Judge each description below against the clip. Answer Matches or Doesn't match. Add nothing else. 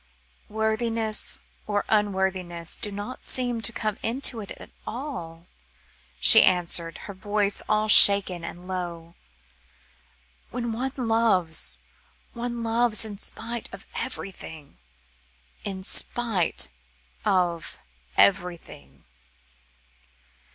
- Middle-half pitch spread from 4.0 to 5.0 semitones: Matches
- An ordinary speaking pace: Doesn't match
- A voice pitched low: Doesn't match